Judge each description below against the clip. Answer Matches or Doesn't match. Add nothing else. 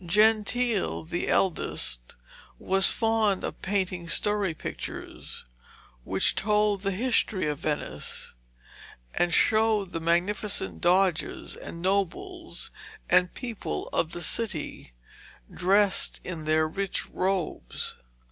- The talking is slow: Matches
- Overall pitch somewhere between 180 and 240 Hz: Matches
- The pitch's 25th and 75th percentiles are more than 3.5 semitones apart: Matches